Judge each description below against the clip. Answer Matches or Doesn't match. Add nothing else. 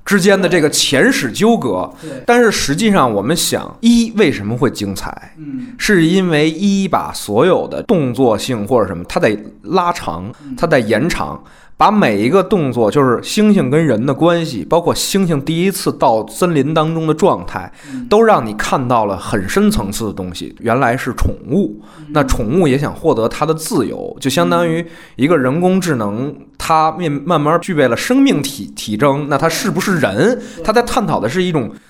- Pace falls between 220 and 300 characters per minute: Matches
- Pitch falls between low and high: Matches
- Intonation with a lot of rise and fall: Matches